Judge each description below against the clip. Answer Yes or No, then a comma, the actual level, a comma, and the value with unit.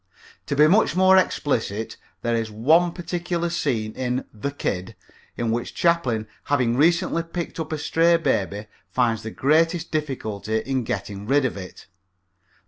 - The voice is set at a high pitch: No, low, 135 Hz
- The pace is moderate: Yes, average, 150 wpm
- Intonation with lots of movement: Yes, wide, 6.9 semitones